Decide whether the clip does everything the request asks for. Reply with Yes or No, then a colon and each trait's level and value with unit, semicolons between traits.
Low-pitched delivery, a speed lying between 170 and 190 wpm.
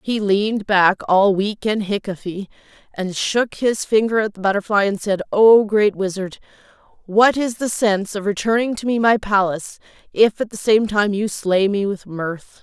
No: high, 205 Hz; average, 185 wpm